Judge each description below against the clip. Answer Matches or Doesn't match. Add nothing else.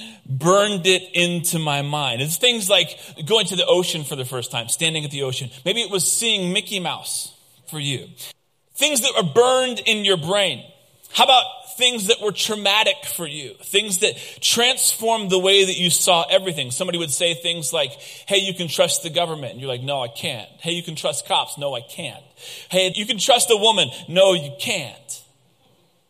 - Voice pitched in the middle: Matches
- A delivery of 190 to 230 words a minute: Matches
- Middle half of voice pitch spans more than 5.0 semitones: Matches